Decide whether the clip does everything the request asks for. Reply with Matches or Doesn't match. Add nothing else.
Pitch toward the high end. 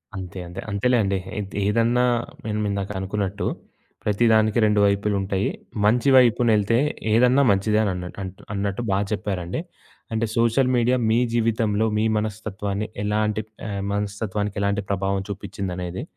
Doesn't match